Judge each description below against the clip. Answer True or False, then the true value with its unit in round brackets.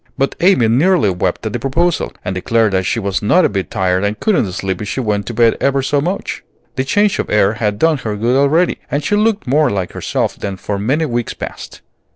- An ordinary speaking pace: False (230 wpm)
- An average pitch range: False (6.7 semitones)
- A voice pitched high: False (115 Hz)